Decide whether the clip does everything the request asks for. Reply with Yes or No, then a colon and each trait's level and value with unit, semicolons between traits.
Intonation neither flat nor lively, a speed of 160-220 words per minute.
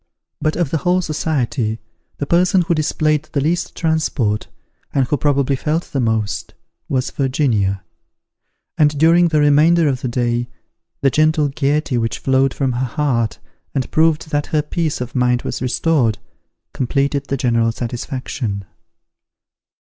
No: average, 3.9 semitones; average, 145 wpm